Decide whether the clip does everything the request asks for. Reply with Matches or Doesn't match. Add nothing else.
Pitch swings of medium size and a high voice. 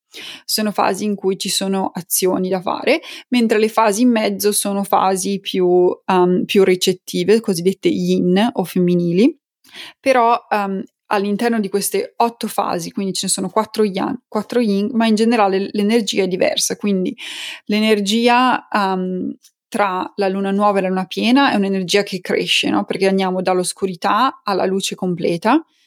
Matches